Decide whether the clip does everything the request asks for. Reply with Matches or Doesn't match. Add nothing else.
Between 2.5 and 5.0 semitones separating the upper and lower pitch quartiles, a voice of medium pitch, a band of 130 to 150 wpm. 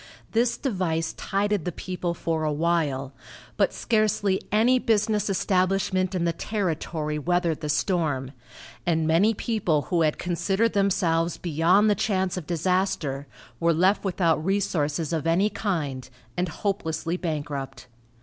Matches